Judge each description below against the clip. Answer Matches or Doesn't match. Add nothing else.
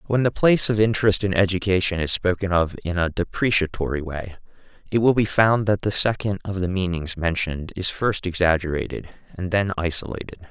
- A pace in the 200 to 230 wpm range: Doesn't match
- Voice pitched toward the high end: Doesn't match